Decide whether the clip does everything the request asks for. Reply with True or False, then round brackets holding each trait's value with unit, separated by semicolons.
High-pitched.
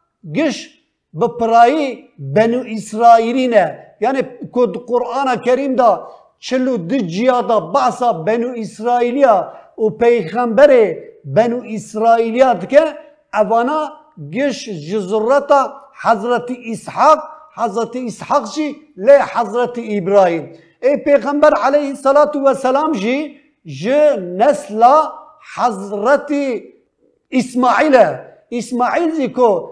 True (250 Hz)